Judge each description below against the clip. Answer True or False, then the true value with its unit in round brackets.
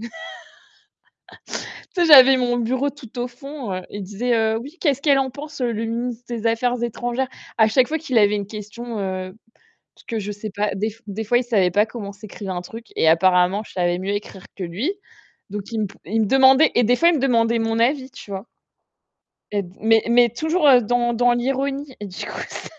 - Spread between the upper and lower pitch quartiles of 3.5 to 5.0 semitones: True (3.8 semitones)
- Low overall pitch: False (230 Hz)